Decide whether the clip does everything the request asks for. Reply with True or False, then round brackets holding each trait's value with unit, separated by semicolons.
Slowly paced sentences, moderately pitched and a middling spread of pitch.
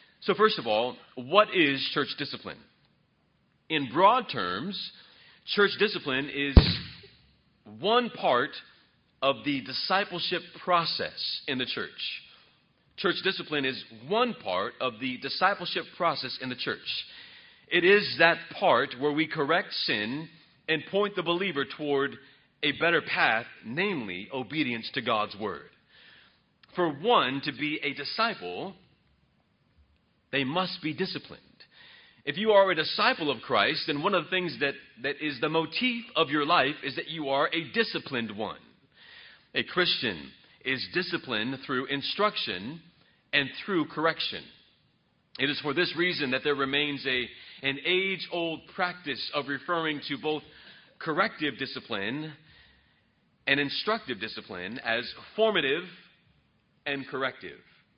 True (130 wpm; 155 Hz; 4.7 semitones)